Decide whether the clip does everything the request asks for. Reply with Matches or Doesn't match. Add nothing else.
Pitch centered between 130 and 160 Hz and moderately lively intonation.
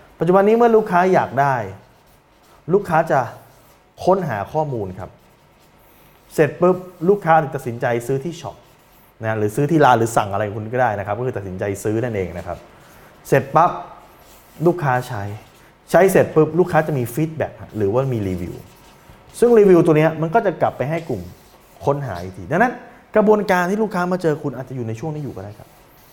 Doesn't match